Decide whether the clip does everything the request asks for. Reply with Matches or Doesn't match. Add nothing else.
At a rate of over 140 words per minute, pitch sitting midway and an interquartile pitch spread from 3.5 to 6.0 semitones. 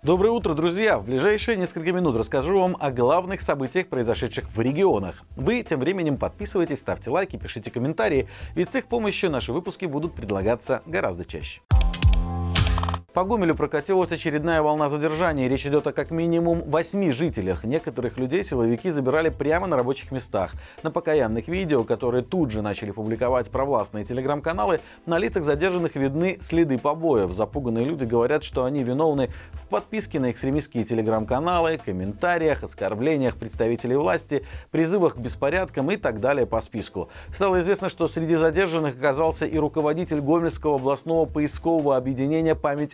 Matches